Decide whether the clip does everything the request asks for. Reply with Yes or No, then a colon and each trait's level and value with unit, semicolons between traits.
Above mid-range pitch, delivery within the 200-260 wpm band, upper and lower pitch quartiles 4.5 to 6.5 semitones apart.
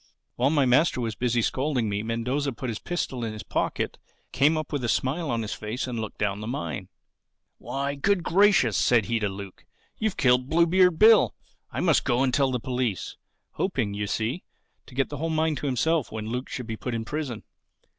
No: low, 125 Hz; fast, 205 wpm; average, 4.8 semitones